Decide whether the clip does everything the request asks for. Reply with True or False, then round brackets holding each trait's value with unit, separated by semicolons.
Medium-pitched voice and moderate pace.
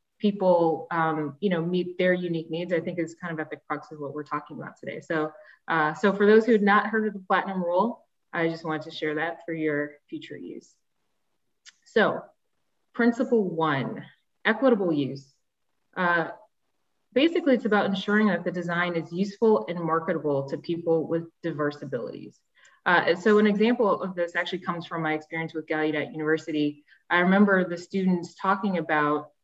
True (170 Hz; 175 wpm)